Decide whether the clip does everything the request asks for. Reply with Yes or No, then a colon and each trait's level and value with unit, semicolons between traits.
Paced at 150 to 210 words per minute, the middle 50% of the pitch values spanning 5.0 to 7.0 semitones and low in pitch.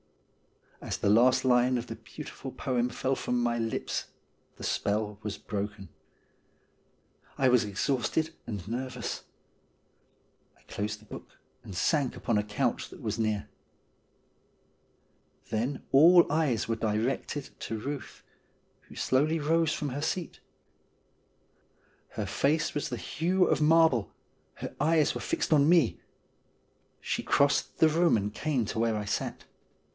No: average, 140 wpm; wide, 5.5 semitones; low, 125 Hz